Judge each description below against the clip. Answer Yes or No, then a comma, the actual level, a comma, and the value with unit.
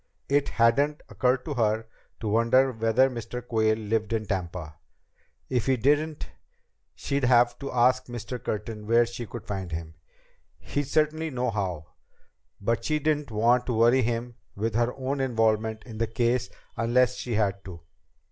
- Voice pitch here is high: No, low, 120 Hz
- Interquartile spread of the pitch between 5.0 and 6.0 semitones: No, average, 2.8 semitones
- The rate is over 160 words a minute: No, average, 155 wpm